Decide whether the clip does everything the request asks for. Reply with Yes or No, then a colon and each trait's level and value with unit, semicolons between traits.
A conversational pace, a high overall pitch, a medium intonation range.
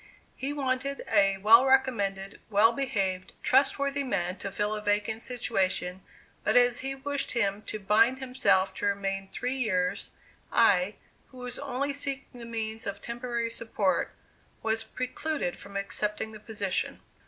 Yes: average, 145 wpm; high, 225 Hz; average, 4.5 semitones